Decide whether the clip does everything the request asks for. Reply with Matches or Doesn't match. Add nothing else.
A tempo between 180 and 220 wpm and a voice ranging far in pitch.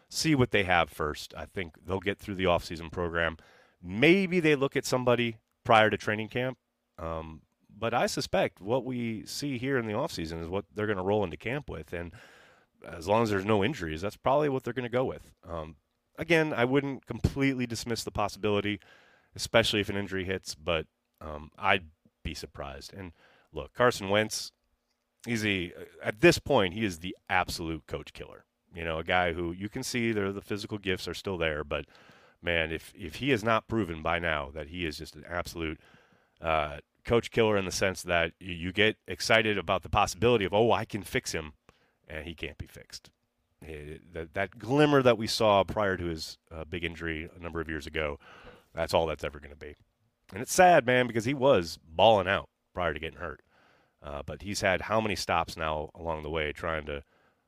Matches